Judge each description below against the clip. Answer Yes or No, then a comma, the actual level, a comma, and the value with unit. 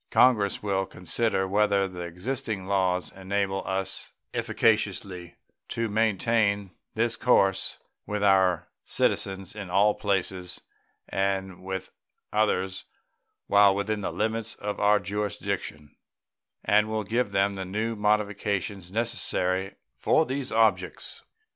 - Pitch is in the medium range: No, low, 100 Hz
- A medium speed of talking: No, slow, 115 wpm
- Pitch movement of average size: No, narrow, 2.0 semitones